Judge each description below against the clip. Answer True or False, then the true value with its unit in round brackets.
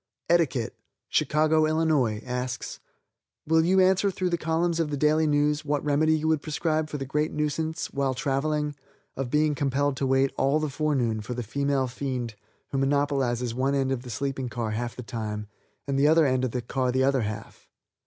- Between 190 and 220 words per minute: True (195 wpm)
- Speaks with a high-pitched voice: False (140 Hz)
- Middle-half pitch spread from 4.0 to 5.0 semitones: False (3.2 semitones)